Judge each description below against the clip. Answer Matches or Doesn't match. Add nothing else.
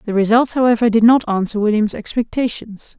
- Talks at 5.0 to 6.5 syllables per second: Matches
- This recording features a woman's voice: Matches